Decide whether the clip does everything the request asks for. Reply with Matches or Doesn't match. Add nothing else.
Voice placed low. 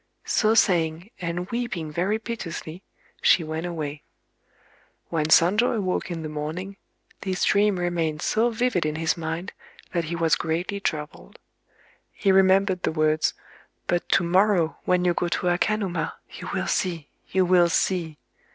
Doesn't match